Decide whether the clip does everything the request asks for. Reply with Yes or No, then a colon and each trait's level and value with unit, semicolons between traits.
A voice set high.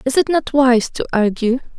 Yes: very high, 255 Hz